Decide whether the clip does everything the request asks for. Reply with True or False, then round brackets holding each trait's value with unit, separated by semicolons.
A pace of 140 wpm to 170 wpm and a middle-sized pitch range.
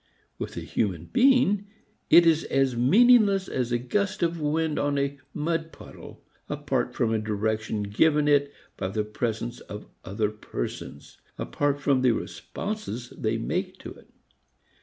False (150 wpm; 7.2 semitones)